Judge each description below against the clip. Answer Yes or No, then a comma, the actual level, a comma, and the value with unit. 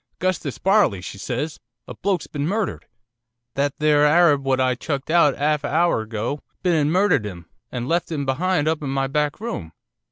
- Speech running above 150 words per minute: Yes, average, 190 wpm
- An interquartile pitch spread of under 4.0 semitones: No, average, 4.3 semitones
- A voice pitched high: No, medium, 145 Hz